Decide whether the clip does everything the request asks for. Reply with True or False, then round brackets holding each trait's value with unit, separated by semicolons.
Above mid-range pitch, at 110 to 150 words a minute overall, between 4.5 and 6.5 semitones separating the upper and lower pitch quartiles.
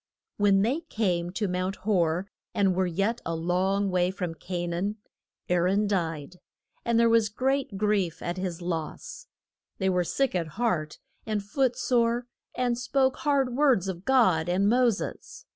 False (195 Hz; 165 wpm; 4.8 semitones)